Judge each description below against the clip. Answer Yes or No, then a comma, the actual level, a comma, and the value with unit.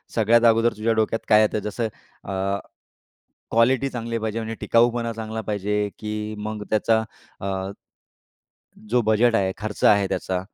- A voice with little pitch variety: Yes, narrow, 1.6 semitones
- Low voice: Yes, low, 110 Hz